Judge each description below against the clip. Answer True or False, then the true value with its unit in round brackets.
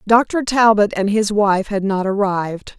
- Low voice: False (205 Hz)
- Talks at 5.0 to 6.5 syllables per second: False (4.2 syllables/s)